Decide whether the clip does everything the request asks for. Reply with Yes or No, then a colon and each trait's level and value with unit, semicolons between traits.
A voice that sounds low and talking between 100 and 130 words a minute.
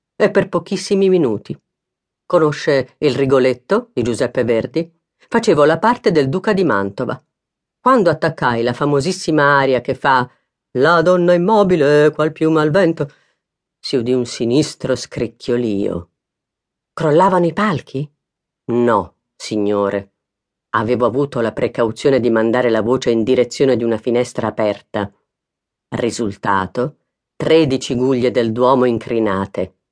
Yes: low, 130 Hz; average, 120 wpm